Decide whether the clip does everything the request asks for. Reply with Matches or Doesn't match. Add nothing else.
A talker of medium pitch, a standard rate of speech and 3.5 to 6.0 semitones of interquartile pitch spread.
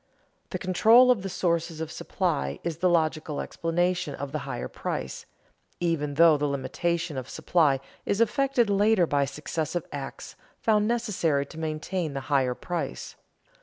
Matches